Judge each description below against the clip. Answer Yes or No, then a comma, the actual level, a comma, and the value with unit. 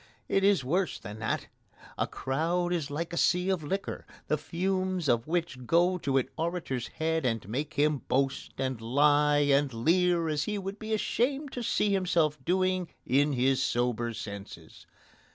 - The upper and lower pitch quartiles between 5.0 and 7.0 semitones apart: Yes, wide, 5.4 semitones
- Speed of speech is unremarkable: Yes, average, 170 wpm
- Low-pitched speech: No, medium, 155 Hz